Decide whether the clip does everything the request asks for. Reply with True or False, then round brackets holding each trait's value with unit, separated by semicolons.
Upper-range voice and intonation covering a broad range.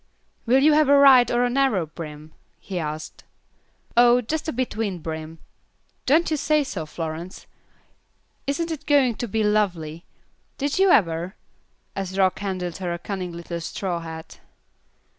True (195 Hz; 7.9 semitones)